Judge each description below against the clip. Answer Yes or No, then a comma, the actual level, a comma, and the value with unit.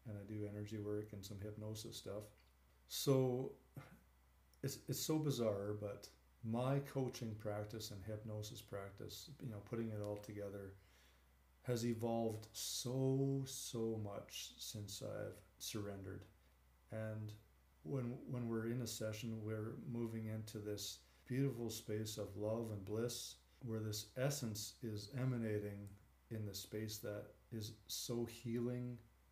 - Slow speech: Yes, slow, 130 wpm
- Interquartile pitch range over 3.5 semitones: No, narrow, 2.5 semitones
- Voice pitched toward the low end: Yes, low, 110 Hz